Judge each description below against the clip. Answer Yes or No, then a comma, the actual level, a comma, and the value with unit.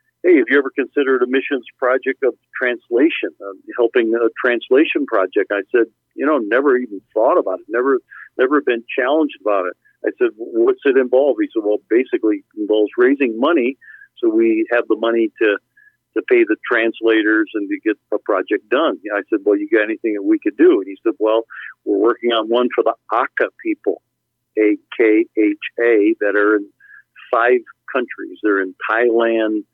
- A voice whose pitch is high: Yes, very high, 335 Hz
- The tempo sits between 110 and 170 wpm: No, average, 190 wpm